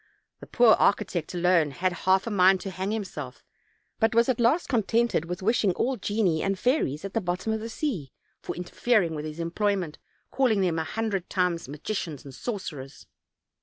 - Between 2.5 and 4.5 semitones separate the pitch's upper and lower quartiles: No, average, 4.9 semitones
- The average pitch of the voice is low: No, high, 190 Hz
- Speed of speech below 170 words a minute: No, average, 180 wpm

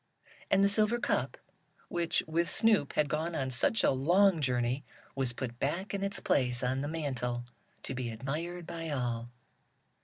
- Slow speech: No, average, 165 wpm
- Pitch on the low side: No, medium, 145 Hz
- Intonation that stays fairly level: No, wide, 5.6 semitones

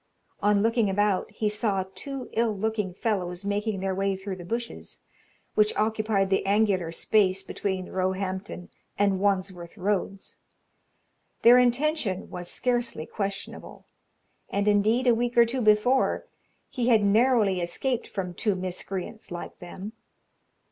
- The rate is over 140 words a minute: No, slow, 135 wpm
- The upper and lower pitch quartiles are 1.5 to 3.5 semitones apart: Yes, average, 3.0 semitones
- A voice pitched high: Yes, high, 205 Hz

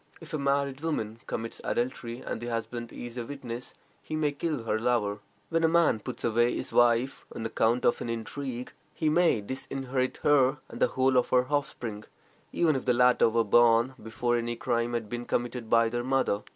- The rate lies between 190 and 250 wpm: Yes, average, 195 wpm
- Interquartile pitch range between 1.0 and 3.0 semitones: Yes, narrow, 2.6 semitones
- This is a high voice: No, low, 120 Hz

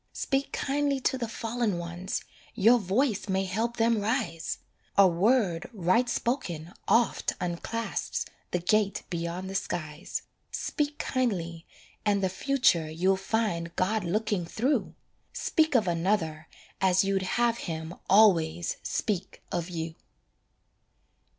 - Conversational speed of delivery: No, slow, 125 wpm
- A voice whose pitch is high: Yes, high, 195 Hz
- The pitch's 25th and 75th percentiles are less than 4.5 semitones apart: No, average, 5.1 semitones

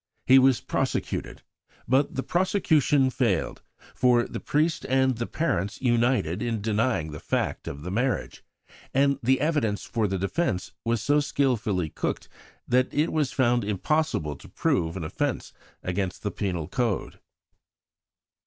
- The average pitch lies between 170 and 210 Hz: No, low, 120 Hz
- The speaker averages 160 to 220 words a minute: No, average, 145 wpm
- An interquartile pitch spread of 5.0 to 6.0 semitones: Yes, wide, 5.5 semitones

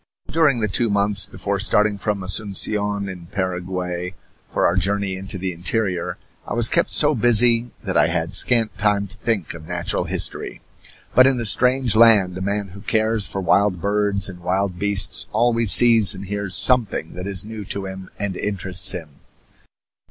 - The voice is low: Yes, low, 100 Hz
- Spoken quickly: No, average, 175 wpm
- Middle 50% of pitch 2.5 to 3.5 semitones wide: Yes, average, 2.9 semitones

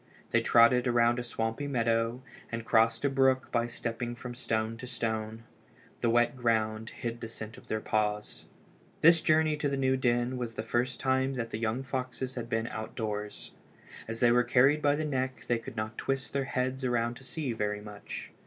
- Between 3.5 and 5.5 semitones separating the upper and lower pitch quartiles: No, narrow, 2.5 semitones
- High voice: No, low, 120 Hz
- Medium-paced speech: Yes, average, 195 wpm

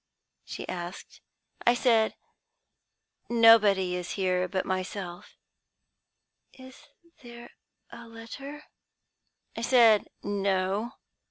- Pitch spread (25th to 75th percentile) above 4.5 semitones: No, average, 4.1 semitones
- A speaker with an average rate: No, slow, 85 wpm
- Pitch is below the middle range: No, high, 215 Hz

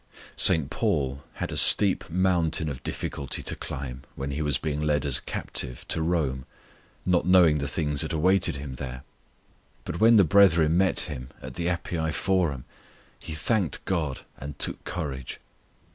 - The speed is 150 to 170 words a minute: Yes, average, 165 wpm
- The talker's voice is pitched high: No, very low, 80 Hz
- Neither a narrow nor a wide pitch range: Yes, average, 4.1 semitones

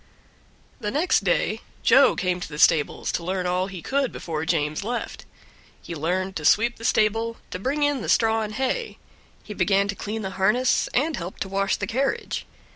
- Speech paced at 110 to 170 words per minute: No, average, 195 wpm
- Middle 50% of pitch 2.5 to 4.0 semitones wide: No, average, 4.6 semitones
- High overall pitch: Yes, high, 200 Hz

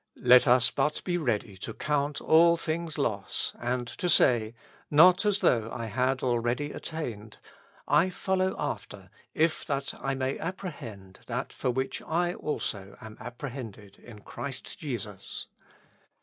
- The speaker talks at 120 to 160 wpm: Yes, average, 150 wpm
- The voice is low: Yes, low, 130 Hz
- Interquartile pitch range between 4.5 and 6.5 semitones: Yes, wide, 5.6 semitones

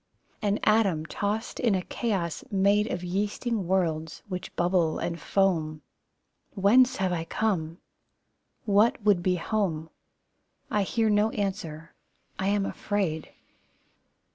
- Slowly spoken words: Yes, slow, 120 wpm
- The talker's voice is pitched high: Yes, high, 195 Hz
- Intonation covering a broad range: No, average, 3.6 semitones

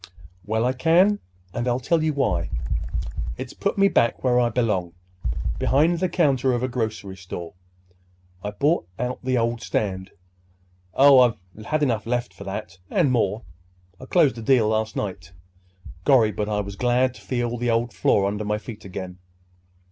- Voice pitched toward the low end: Yes, low, 120 Hz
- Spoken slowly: No, average, 165 wpm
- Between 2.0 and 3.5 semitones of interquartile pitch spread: No, average, 4.0 semitones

